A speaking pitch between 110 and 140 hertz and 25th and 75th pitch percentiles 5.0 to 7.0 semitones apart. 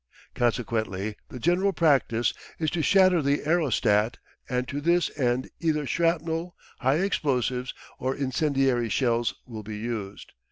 Yes: low, 135 Hz; wide, 5.4 semitones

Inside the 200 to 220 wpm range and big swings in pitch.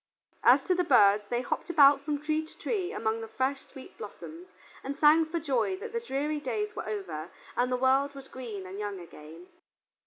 Yes: fast, 205 wpm; wide, 6.3 semitones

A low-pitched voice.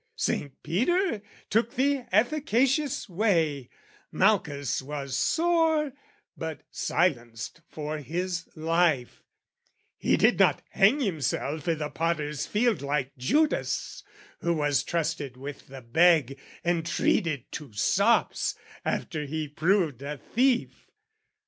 No: medium, 165 Hz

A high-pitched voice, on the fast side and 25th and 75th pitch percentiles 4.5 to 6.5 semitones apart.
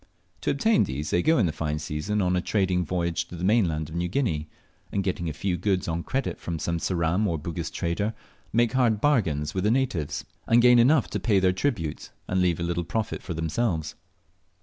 No: very low, 90 Hz; fast, 215 wpm; average, 4.8 semitones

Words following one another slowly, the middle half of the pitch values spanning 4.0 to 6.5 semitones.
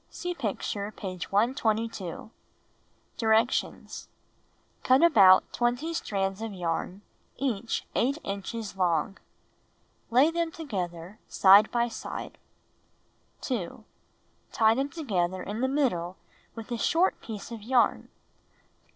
Yes: slow, 110 wpm; average, 4.9 semitones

